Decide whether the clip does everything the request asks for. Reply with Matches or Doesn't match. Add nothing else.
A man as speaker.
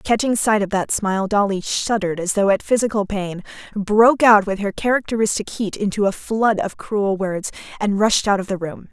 Doesn't match